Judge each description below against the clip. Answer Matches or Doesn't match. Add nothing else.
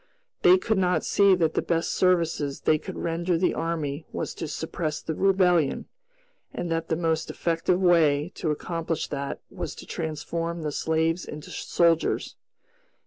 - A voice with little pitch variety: Matches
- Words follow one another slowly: Doesn't match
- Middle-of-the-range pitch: Matches